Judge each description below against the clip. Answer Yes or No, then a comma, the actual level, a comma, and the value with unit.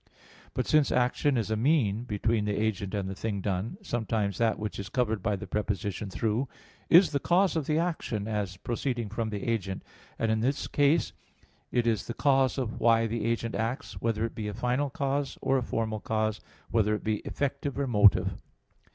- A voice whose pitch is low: Yes, low, 115 Hz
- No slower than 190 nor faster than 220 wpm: Yes, average, 195 wpm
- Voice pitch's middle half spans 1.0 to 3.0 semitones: No, average, 4.0 semitones